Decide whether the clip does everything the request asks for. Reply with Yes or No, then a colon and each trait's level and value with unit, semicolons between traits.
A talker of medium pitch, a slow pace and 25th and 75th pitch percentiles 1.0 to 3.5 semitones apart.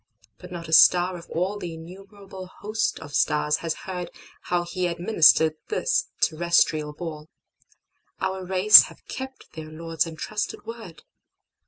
Yes: medium, 175 Hz; slow, 125 wpm; average, 3.0 semitones